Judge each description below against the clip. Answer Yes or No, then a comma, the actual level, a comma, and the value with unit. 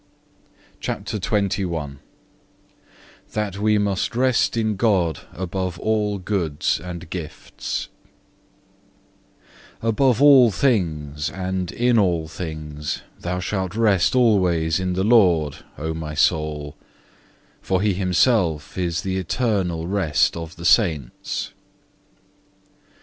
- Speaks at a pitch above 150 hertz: No, very low, 90 Hz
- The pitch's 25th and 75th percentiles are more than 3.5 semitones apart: Yes, average, 4.4 semitones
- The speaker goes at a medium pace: No, slow, 105 wpm